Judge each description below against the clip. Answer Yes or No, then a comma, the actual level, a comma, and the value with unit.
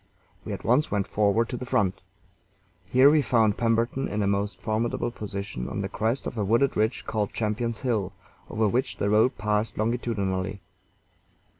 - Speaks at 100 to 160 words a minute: No, average, 170 wpm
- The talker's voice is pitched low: Yes, low, 110 Hz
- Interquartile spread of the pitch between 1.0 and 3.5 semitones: Yes, average, 2.8 semitones